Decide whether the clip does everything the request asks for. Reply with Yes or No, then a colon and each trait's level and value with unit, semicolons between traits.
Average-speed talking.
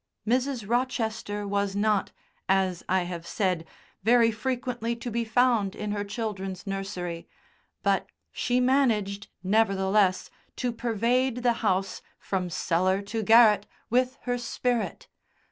No: slow, 125 wpm